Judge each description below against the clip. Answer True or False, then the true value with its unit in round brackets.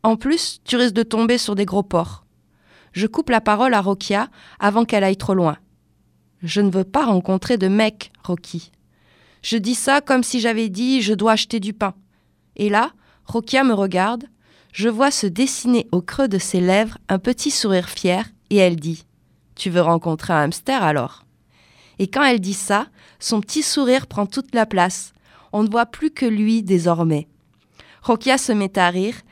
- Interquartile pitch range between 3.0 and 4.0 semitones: False (4.6 semitones)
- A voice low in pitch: False (210 Hz)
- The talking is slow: False (190 wpm)